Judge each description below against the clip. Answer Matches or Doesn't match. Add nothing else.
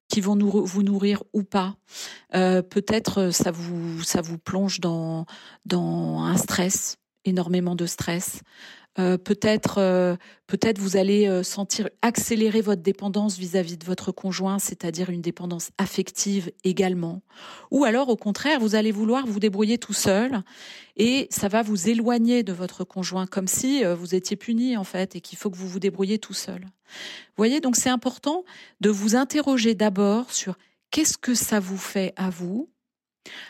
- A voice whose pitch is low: Doesn't match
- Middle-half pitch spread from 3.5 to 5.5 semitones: Doesn't match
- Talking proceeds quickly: Doesn't match